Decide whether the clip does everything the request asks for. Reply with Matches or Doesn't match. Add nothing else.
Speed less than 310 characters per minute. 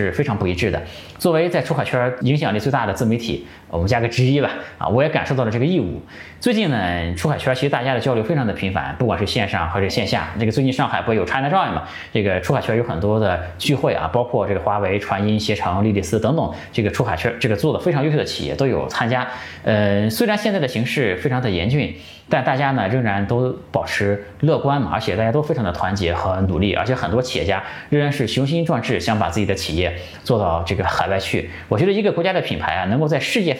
Doesn't match